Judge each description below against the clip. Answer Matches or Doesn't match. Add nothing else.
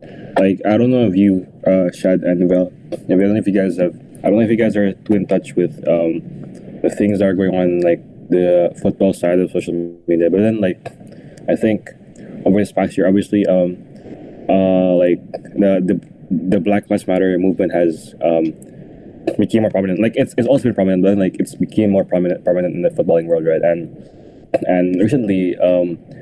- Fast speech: Matches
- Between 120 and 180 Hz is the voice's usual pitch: Doesn't match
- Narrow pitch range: Matches